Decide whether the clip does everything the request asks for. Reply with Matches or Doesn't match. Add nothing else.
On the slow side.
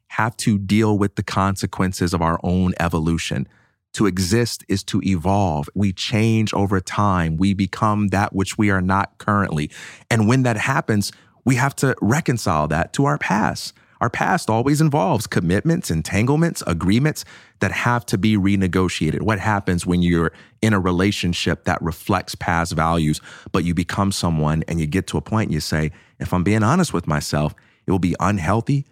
Doesn't match